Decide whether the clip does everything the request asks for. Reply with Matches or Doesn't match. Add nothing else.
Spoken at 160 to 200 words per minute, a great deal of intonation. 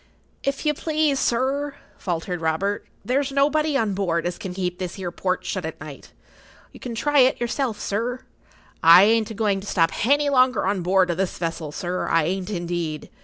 Matches